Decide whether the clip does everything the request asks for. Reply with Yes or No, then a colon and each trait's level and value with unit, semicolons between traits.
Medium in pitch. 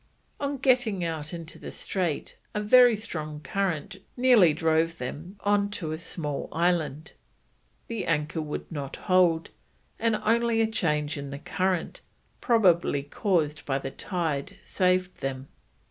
Yes: medium, 170 Hz